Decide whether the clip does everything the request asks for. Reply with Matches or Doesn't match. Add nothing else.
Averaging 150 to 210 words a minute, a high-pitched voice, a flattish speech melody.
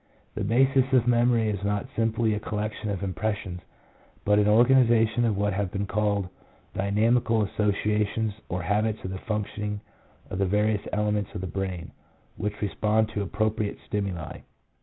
Doesn't match